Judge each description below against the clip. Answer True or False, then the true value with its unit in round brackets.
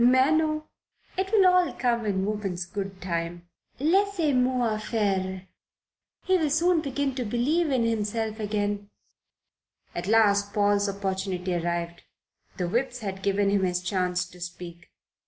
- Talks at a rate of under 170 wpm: True (140 wpm)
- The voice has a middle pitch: False (205 Hz)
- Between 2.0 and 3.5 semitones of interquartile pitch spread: False (5.5 semitones)